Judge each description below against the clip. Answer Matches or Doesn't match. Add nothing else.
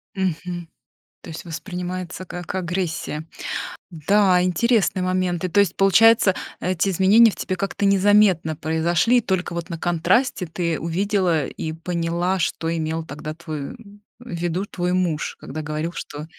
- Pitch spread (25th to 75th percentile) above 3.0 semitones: Doesn't match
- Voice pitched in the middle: Matches